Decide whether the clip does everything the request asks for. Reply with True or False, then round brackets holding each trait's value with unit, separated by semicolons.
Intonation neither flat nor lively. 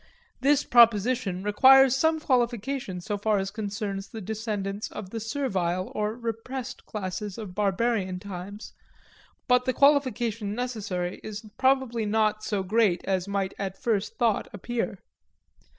True (3.4 semitones)